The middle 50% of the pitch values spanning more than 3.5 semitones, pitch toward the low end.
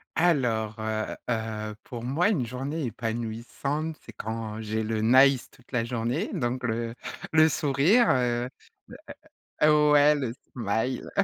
Yes: average, 4.2 semitones; low, 120 Hz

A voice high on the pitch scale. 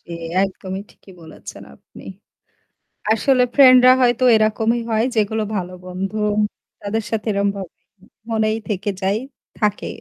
Yes: high, 215 Hz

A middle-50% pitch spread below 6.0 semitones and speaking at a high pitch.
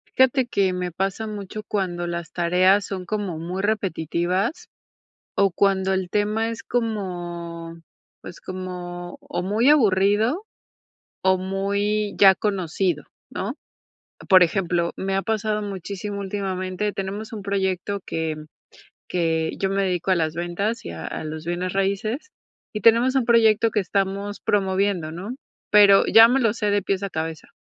Yes: average, 2.8 semitones; high, 195 Hz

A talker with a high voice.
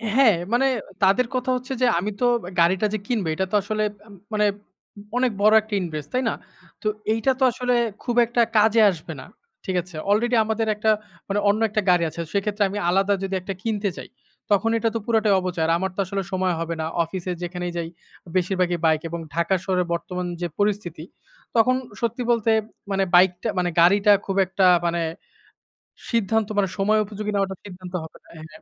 Yes: high, 200 Hz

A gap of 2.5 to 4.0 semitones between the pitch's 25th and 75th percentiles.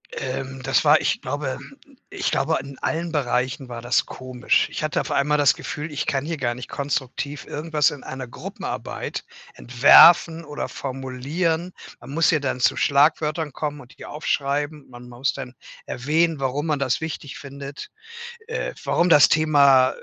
Yes: average, 2.8 semitones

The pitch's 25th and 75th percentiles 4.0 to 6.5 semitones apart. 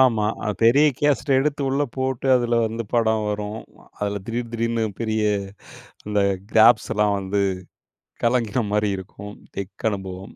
No: average, 2.8 semitones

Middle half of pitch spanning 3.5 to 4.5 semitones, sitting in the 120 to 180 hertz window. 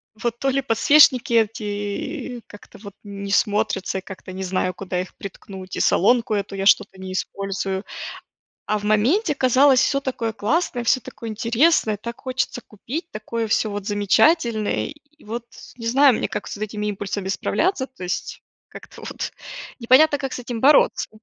No: average, 4.2 semitones; high, 220 Hz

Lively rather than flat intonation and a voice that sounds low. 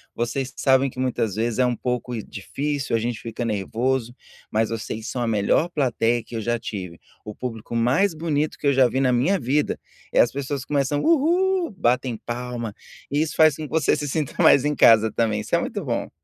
No: average, 4.0 semitones; low, 125 Hz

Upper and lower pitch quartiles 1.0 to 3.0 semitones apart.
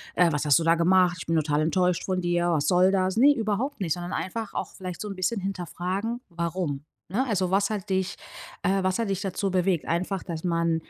Yes: narrow, 2.5 semitones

